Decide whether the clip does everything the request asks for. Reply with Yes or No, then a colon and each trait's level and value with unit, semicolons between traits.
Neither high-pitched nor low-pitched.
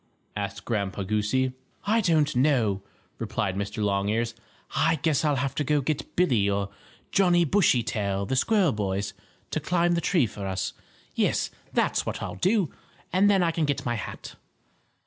No: low, 130 Hz